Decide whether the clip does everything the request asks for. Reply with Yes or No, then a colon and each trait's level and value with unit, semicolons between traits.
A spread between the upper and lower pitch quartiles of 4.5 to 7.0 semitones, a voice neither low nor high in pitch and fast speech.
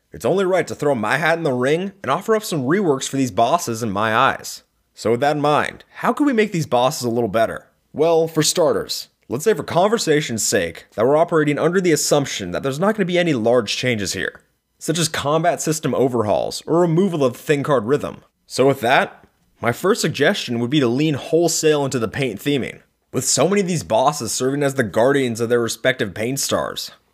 Yes: average, 4.8 semitones; medium, 145 Hz; fast, 220 wpm